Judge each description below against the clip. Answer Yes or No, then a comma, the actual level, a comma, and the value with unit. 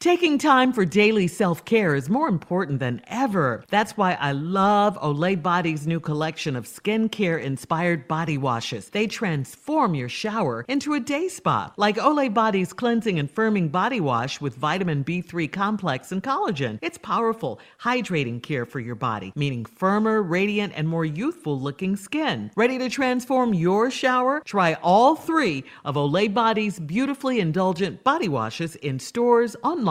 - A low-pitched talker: No, high, 190 Hz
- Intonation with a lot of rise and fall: Yes, wide, 7.3 semitones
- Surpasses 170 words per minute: No, average, 155 wpm